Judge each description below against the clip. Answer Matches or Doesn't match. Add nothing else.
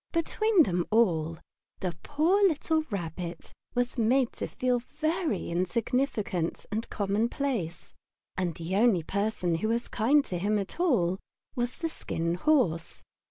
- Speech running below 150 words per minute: Matches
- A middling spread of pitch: Doesn't match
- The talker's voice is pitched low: Doesn't match